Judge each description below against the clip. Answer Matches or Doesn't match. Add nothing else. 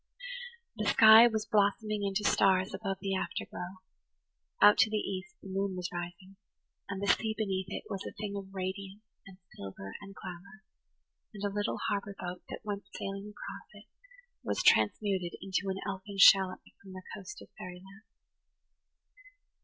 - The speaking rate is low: Doesn't match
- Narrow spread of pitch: Matches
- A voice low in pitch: Doesn't match